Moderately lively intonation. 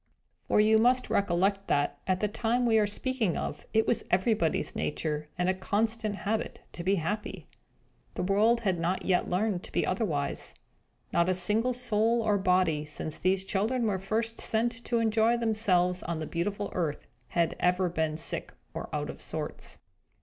Yes: average, 3.8 semitones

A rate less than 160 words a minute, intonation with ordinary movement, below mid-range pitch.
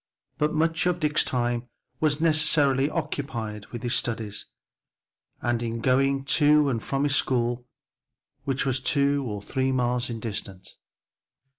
Yes: slow, 135 wpm; average, 3.5 semitones; low, 130 Hz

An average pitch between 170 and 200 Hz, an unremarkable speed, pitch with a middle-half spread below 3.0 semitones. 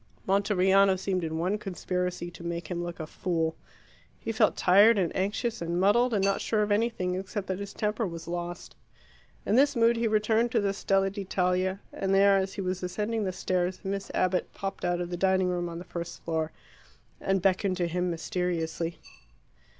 Yes: high, 190 Hz; average, 190 wpm; narrow, 2.4 semitones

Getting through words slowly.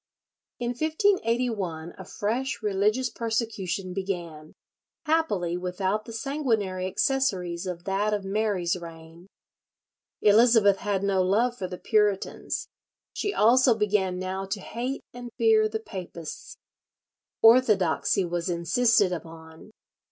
Yes: slow, 115 wpm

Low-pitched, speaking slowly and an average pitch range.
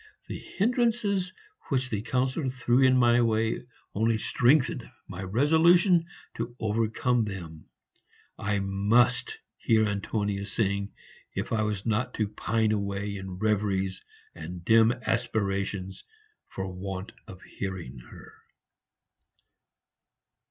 Yes: low, 110 Hz; slow, 110 wpm; average, 4.2 semitones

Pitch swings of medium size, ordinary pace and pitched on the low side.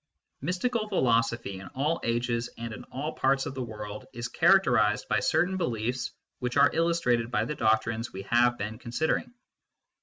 Yes: average, 4.7 semitones; average, 170 wpm; low, 120 Hz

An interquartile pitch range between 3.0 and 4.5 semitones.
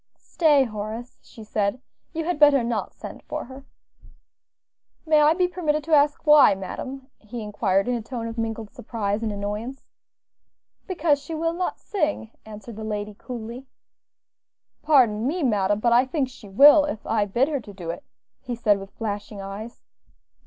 No: wide, 5.6 semitones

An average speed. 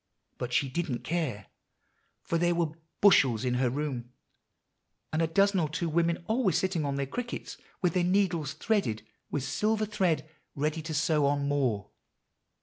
Yes: average, 160 wpm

